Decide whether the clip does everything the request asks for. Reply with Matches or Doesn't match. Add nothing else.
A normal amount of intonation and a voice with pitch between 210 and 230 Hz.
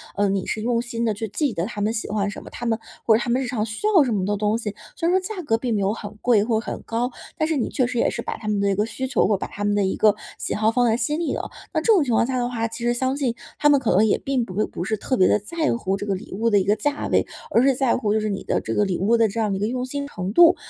Matches